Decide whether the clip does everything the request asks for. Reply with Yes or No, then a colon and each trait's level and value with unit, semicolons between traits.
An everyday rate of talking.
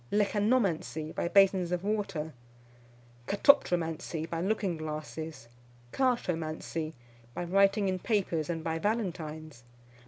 No: slow, 100 wpm